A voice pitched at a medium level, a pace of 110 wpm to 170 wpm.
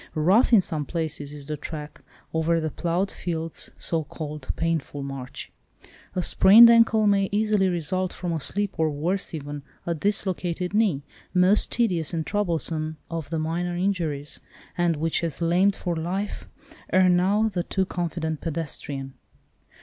Yes: medium, 170 Hz; average, 150 wpm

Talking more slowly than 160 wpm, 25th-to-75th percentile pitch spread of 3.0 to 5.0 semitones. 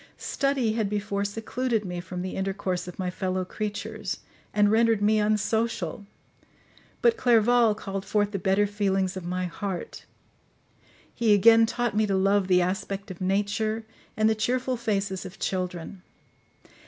No: average, 150 wpm; narrow, 2.6 semitones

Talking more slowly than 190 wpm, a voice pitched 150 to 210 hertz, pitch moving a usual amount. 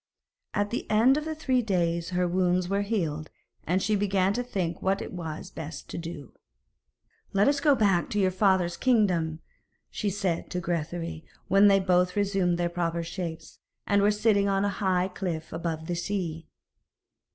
Yes: average, 180 wpm; medium, 185 Hz; average, 3.1 semitones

